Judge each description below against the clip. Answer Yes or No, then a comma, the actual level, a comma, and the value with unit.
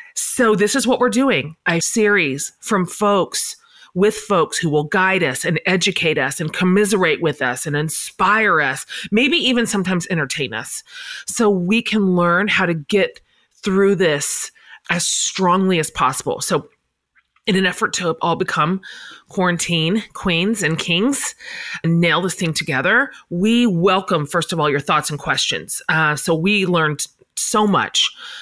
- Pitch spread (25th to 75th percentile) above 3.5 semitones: Yes, average, 4.5 semitones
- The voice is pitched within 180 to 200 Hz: Yes, medium, 185 Hz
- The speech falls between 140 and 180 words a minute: Yes, average, 160 wpm